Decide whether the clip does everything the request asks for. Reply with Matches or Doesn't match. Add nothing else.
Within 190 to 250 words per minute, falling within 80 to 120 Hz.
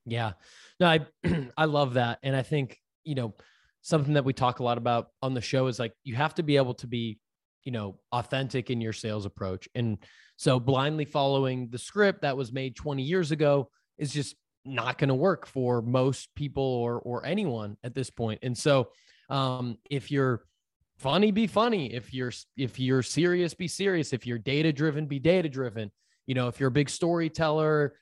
Doesn't match